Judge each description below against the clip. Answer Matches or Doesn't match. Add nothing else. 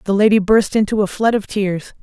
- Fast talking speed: Matches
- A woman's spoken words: Matches